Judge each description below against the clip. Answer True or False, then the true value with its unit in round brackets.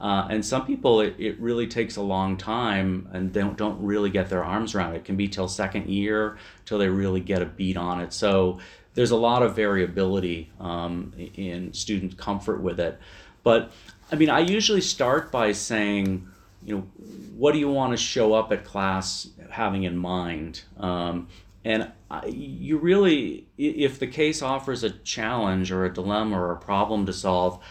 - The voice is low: True (100 Hz)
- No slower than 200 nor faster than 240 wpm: False (190 wpm)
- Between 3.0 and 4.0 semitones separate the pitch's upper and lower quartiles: True (3.3 semitones)